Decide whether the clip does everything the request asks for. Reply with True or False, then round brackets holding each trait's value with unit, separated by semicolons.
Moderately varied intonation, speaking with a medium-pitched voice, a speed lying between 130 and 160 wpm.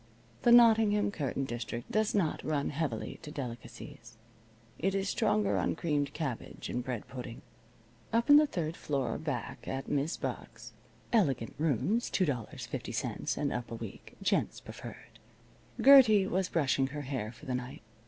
False (7.9 semitones; 145 Hz; 150 wpm)